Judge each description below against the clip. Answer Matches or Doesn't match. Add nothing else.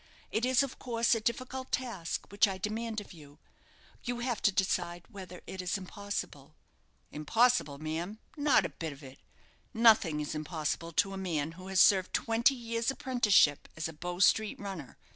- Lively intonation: Matches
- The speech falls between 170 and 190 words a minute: Matches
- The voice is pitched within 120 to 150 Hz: Doesn't match